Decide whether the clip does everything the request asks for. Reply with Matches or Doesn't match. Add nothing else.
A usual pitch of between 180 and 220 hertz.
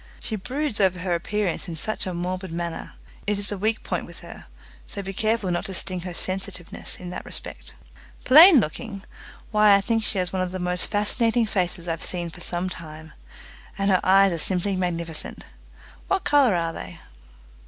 Matches